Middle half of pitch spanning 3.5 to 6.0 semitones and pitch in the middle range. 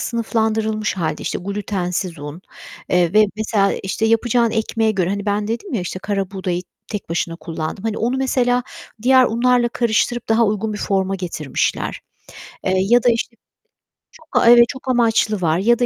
No: average, 3.8 semitones; high, 215 Hz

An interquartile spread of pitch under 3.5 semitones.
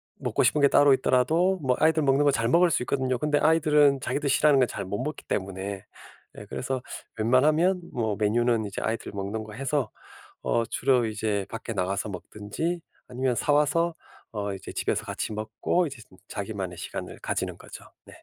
No: wide, 5.6 semitones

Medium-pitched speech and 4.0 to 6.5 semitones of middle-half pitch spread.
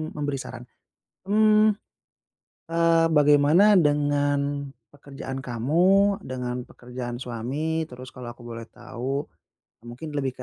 Yes: medium, 145 Hz; average, 4.3 semitones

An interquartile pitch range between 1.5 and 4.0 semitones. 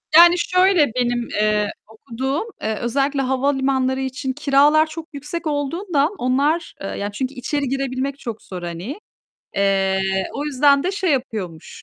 No: average, 4.4 semitones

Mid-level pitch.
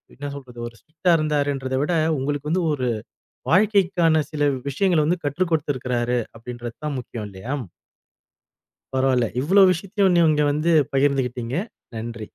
Yes: medium, 145 Hz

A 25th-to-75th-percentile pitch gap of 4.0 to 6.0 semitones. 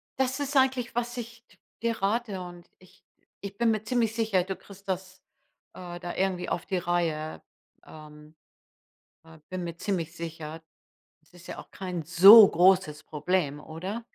Yes: average, 4.6 semitones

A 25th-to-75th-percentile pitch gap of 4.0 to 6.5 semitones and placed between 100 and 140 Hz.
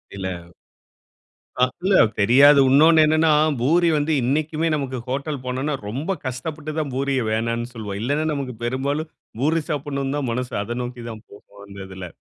Yes: average, 4.3 semitones; low, 135 Hz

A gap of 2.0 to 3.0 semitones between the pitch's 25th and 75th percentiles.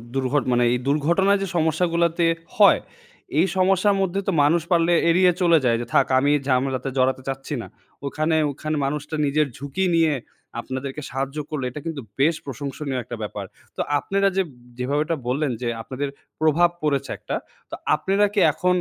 No: average, 4.1 semitones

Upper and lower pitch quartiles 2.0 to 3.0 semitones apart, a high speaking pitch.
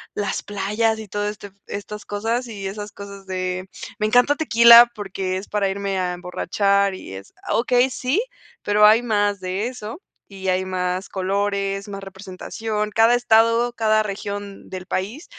Yes: narrow, 2.6 semitones; high, 205 Hz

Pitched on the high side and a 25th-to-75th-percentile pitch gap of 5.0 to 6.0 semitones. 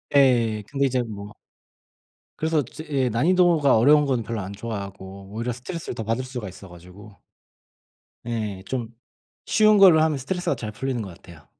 No: low, 120 Hz; wide, 5.4 semitones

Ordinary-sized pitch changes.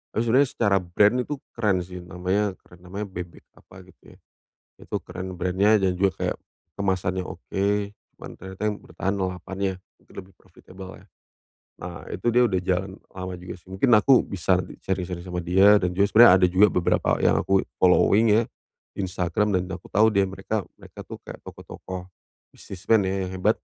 No: narrow, 1.9 semitones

